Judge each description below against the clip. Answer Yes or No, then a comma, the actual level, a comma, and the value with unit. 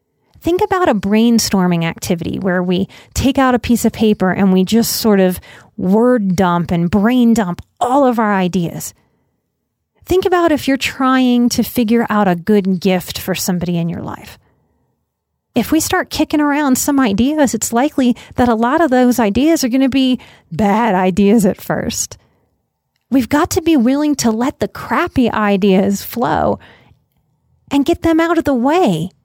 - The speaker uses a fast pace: No, average, 170 wpm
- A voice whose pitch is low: No, high, 235 Hz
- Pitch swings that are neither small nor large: No, wide, 5.8 semitones